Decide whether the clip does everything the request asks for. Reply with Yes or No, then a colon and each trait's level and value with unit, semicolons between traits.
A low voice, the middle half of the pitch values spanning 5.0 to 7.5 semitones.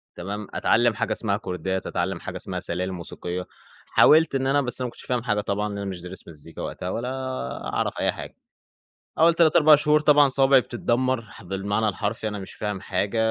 Yes: low, 105 Hz; wide, 5.5 semitones